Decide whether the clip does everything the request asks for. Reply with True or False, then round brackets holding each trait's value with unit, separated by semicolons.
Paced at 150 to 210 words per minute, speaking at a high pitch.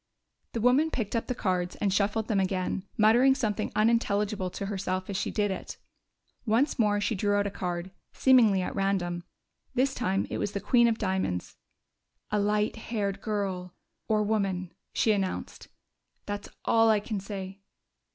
True (165 wpm; 205 Hz)